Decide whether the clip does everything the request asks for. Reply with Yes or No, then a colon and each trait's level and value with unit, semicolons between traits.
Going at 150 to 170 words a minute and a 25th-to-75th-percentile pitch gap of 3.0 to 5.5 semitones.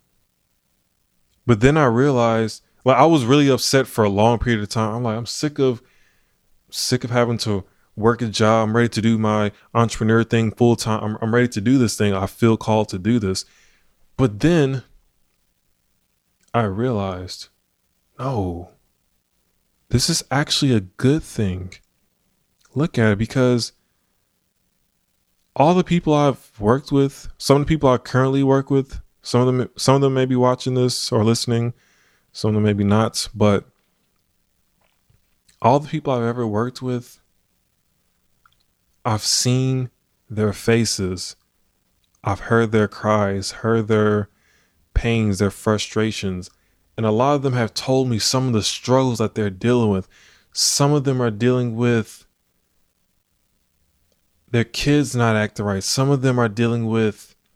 Yes: average, 155 wpm; average, 3.9 semitones